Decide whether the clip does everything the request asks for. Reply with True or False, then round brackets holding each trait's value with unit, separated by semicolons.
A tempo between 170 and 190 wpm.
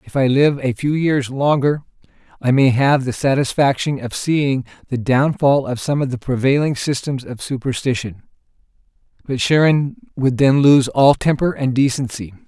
False (160 wpm)